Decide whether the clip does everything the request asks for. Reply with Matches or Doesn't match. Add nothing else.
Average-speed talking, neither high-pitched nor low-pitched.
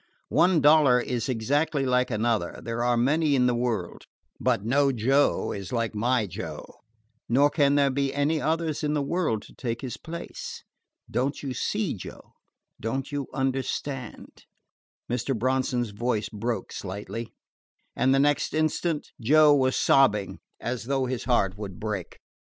Doesn't match